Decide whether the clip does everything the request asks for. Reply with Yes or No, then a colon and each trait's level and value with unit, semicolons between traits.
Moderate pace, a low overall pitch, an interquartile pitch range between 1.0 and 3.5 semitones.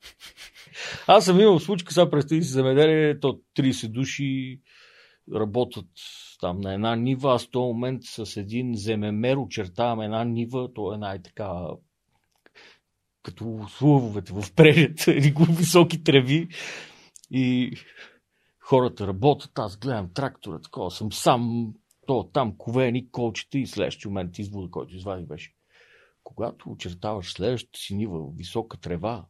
No: average, 125 wpm; low, 120 Hz; average, 4.7 semitones